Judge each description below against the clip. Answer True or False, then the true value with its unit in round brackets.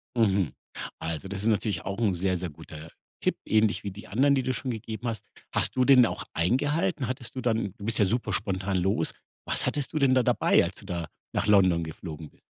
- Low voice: True (105 Hz)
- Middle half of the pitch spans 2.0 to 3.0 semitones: False (5.0 semitones)